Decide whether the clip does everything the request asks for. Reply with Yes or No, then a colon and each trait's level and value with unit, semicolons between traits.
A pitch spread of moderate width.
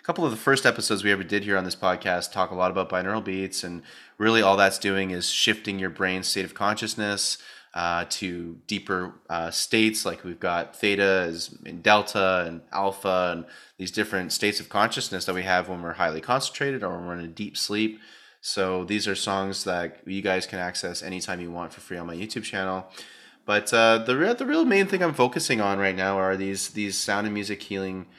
No: narrow, 2.2 semitones